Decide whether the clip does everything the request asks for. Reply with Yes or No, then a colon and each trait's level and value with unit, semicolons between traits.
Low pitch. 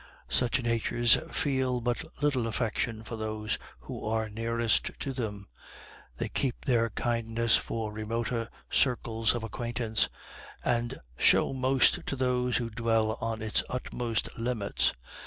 Yes: low, 115 Hz